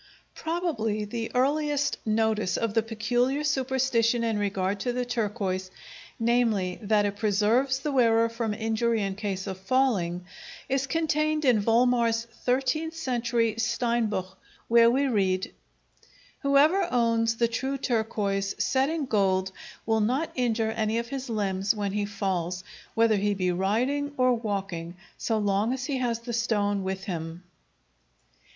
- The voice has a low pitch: No, high, 230 Hz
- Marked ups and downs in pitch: No, average, 3.8 semitones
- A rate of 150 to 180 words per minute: No, average, 140 wpm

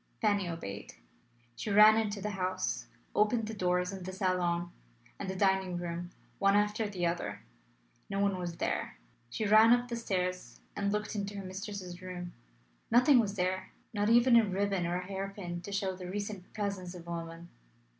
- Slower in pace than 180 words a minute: No, average, 185 wpm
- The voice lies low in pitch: No, high, 195 Hz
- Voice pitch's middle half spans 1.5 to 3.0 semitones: Yes, narrow, 2.5 semitones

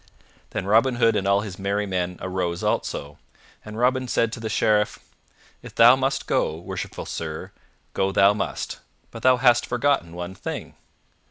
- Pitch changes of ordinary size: Yes, average, 4.5 semitones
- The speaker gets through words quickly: No, average, 165 wpm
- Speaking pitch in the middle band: No, low, 105 Hz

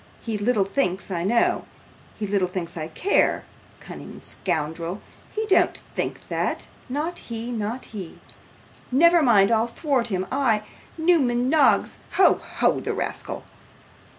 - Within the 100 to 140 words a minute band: Yes, slow, 135 wpm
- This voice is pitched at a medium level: No, high, 230 Hz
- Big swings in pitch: Yes, wide, 6.2 semitones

